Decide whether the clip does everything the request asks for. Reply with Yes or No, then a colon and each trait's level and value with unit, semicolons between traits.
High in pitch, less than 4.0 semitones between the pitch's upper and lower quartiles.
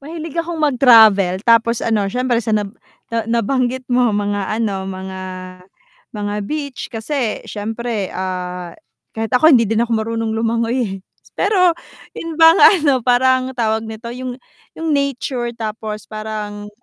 Yes: high, 230 Hz; average, 3.5 semitones